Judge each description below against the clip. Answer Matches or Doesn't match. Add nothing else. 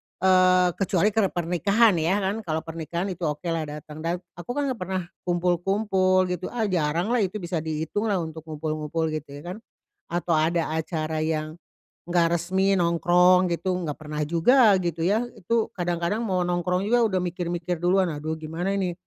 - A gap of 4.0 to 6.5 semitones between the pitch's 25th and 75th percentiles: Doesn't match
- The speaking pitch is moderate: Matches